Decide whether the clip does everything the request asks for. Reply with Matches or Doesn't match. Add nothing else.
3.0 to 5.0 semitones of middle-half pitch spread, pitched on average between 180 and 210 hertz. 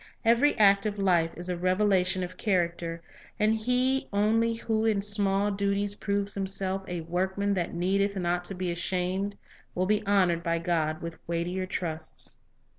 Doesn't match